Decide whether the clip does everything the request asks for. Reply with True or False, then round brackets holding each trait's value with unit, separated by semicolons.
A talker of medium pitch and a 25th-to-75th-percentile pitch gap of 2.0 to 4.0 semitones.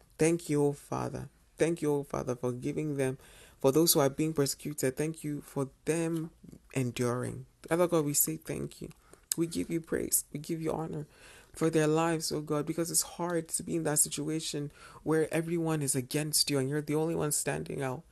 True (150 Hz; 2.6 semitones)